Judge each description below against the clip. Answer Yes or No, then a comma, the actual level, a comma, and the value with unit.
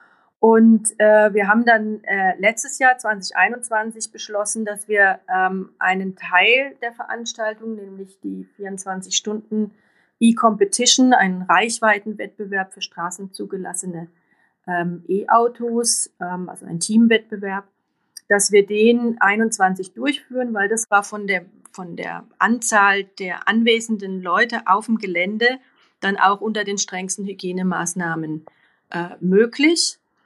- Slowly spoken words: Yes, slow, 115 wpm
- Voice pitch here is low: No, high, 205 Hz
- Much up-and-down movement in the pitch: No, average, 3.1 semitones